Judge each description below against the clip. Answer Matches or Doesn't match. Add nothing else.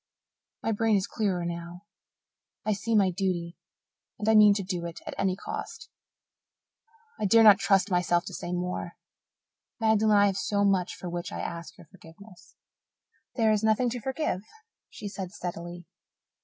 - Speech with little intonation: Doesn't match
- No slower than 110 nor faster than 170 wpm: Matches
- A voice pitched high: Matches